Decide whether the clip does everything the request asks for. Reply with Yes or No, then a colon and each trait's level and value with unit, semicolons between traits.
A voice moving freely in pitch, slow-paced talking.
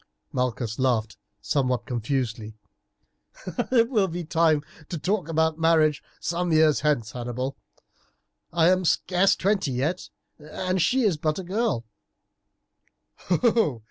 Yes: wide, 6.0 semitones; slow, 115 wpm